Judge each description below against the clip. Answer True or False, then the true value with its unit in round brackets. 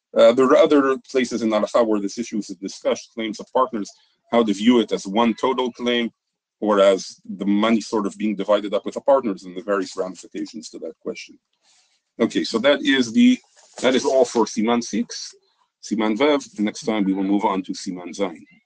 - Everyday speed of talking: False (210 wpm)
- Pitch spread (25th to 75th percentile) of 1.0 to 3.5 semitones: False (4.0 semitones)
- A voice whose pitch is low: True (115 Hz)